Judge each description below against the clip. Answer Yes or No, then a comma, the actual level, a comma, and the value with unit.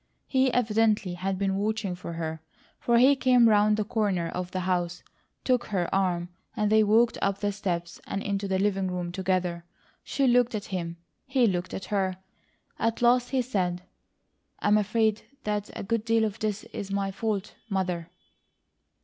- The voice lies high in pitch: Yes, high, 200 Hz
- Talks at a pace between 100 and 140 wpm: No, average, 175 wpm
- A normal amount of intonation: Yes, average, 3.3 semitones